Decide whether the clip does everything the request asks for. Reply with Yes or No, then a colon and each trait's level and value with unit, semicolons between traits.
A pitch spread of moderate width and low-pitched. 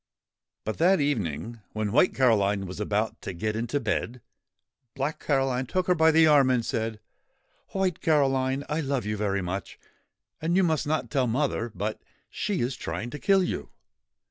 No: wide, 6.0 semitones; low, 130 Hz